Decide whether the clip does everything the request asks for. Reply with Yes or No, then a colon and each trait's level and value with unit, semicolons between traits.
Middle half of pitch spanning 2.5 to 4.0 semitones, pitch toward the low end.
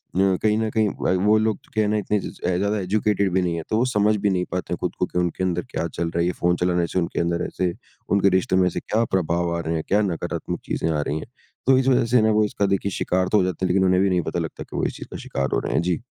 Yes: average, 3.2 semitones; very low, 95 Hz